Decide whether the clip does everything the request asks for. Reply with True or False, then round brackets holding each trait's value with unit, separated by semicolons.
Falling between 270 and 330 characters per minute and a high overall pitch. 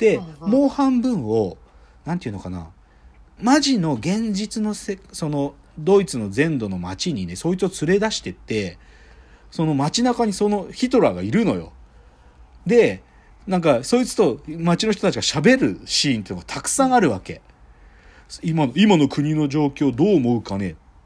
False (310 characters per minute; 150 Hz)